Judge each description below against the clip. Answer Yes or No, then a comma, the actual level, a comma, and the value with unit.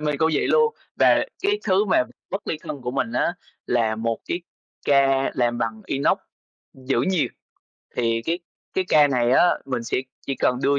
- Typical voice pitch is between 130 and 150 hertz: Yes, low, 135 Hz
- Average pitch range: No, wide, 5.9 semitones